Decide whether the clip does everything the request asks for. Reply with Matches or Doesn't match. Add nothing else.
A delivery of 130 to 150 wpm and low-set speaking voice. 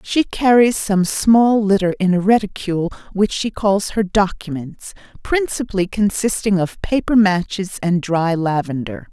Doesn't match